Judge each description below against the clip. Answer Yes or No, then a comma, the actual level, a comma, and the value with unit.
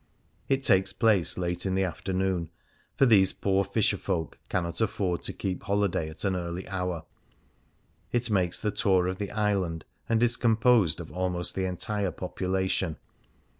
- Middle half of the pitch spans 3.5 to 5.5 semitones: No, narrow, 2.6 semitones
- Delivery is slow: No, average, 160 wpm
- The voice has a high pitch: No, very low, 95 Hz